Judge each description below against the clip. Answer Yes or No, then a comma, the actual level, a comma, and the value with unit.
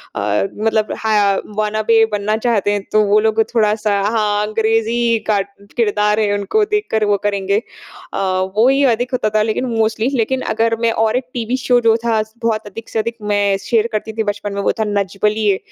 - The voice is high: Yes, high, 215 Hz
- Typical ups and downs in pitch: No, narrow, 1.6 semitones